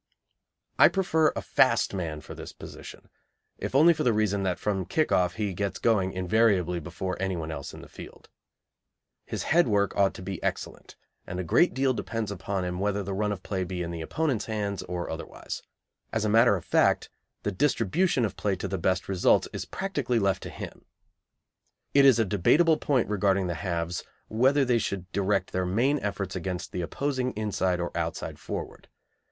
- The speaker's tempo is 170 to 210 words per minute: Yes, average, 190 wpm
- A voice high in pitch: No, low, 100 Hz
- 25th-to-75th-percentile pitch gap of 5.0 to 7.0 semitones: No, average, 4.1 semitones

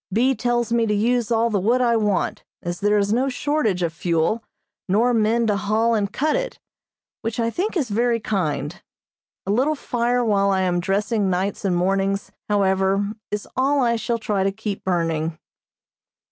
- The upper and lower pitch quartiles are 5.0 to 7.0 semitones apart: No, average, 3.5 semitones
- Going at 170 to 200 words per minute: Yes, average, 180 wpm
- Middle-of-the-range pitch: No, high, 210 Hz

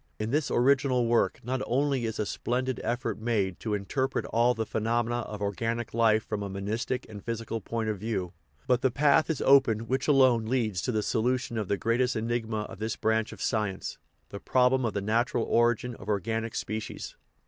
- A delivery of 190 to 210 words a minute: Yes, average, 200 wpm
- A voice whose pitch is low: Yes, low, 115 Hz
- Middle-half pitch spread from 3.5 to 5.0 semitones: No, narrow, 2.6 semitones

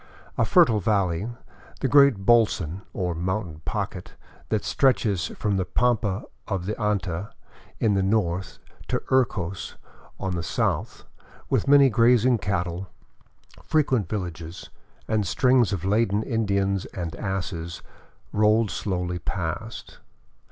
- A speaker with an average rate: No, slow, 115 wpm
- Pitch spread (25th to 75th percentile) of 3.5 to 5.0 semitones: Yes, average, 3.9 semitones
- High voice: No, low, 100 Hz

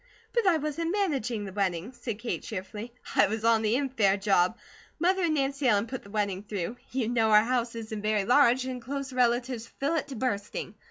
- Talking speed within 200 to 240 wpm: Yes, fast, 205 wpm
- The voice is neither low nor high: No, high, 235 Hz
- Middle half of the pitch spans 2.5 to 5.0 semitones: Yes, average, 4.3 semitones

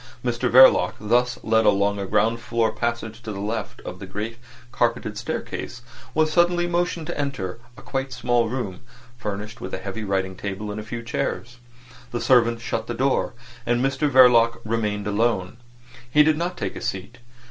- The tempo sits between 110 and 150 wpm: No, average, 180 wpm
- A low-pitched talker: Yes, low, 115 Hz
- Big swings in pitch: No, average, 3.0 semitones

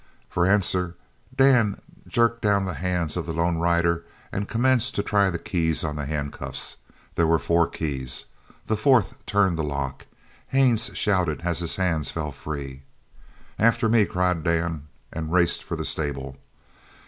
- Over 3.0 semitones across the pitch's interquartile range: Yes, average, 4.5 semitones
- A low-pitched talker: Yes, very low, 85 Hz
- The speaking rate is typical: Yes, average, 160 wpm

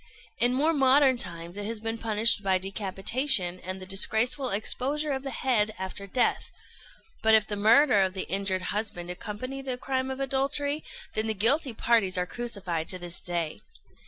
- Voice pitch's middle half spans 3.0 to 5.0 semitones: No, wide, 5.5 semitones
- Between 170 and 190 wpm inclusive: Yes, average, 175 wpm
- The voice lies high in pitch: Yes, high, 220 Hz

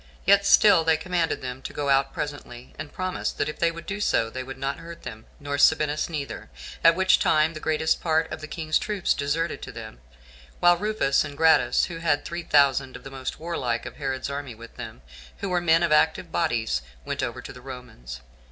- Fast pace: Yes, fast, 215 wpm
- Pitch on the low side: No, medium, 155 Hz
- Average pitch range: Yes, average, 3.8 semitones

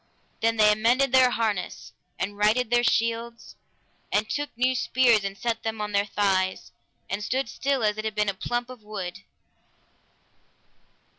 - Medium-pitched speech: No, high, 220 Hz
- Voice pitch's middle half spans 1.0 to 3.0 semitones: Yes, narrow, 2.6 semitones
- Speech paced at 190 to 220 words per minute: No, average, 160 wpm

